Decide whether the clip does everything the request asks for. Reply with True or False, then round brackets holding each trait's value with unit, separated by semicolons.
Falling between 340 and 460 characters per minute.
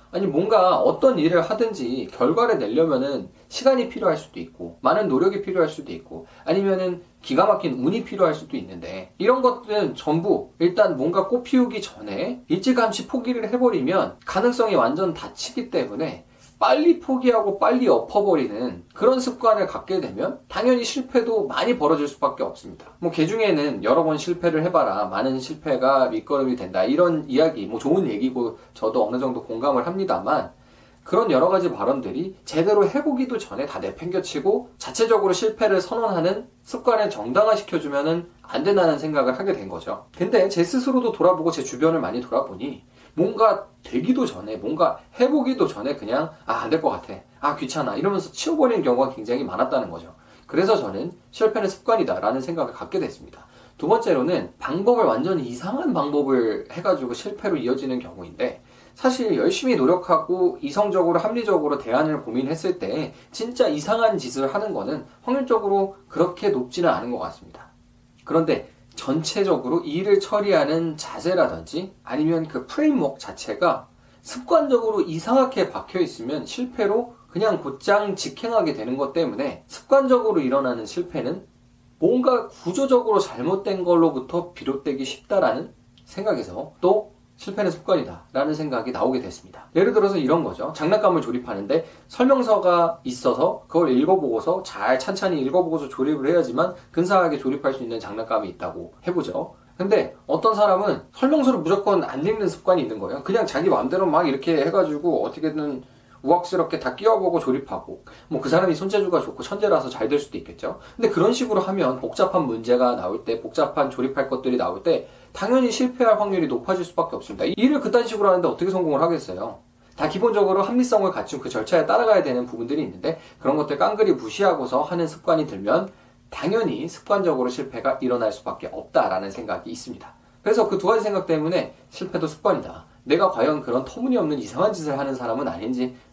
True (390 characters per minute)